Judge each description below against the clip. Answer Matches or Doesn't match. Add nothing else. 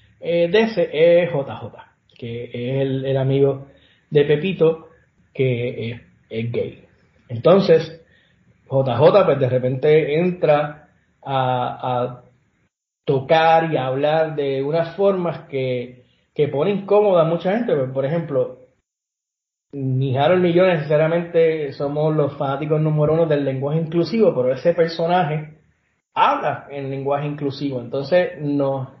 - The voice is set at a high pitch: Doesn't match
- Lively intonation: Doesn't match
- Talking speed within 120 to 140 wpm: Matches